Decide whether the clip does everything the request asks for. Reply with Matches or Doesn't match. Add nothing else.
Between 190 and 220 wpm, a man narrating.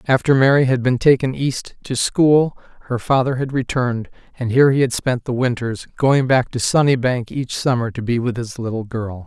Matches